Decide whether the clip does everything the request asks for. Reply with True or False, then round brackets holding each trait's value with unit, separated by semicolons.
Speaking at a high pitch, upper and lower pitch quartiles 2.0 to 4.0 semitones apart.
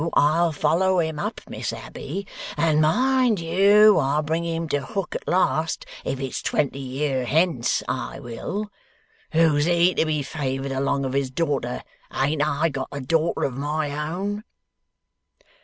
False (155 Hz; 3.6 semitones)